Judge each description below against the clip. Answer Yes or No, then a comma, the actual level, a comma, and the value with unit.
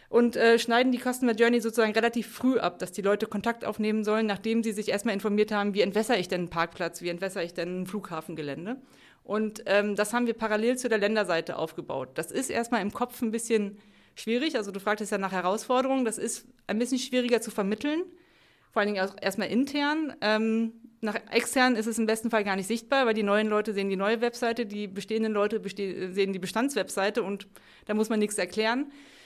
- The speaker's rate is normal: No, fast, 215 wpm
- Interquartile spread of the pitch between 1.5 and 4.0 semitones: Yes, narrow, 2.6 semitones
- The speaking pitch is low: No, high, 220 Hz